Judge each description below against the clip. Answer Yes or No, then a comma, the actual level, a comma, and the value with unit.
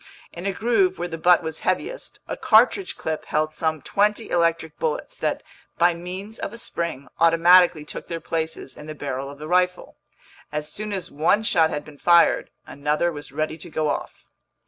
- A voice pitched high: No, medium, 170 Hz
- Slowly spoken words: No, average, 190 wpm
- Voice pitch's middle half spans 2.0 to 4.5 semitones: Yes, average, 3.3 semitones